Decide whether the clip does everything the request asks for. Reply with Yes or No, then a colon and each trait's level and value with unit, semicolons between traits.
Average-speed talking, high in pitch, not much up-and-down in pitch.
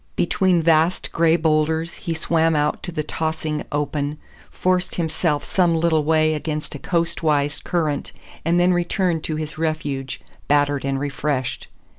No: average, 150 wpm; medium, 155 Hz; narrow, 2.1 semitones